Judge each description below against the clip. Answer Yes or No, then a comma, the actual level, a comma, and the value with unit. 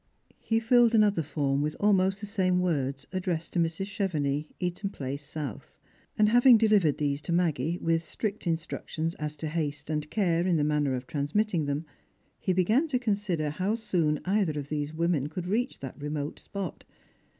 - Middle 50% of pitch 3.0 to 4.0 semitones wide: No, average, 5.0 semitones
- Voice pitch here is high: No, medium, 165 Hz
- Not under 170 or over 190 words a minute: Yes, average, 175 wpm